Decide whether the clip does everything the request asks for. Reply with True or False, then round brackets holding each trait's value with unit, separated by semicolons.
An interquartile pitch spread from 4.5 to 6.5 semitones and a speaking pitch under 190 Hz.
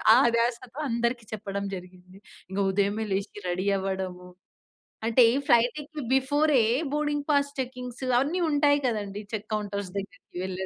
False (5.2 semitones; 225 Hz)